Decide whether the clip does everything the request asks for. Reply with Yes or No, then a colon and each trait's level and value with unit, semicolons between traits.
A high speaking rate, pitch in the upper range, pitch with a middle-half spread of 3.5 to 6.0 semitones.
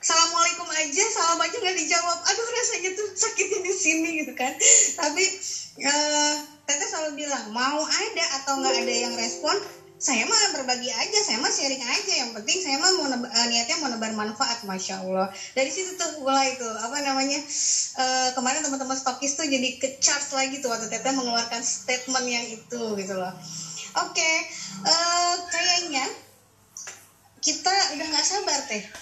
Yes: fast, 170 wpm; very high, 285 Hz; average, 5.3 semitones